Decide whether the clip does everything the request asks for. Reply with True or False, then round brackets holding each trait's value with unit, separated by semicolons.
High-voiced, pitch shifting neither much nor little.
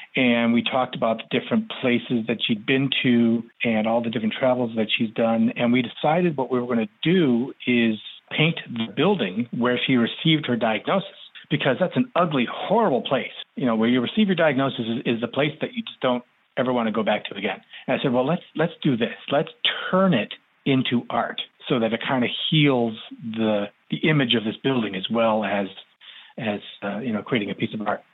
False (125 Hz; 3.9 semitones)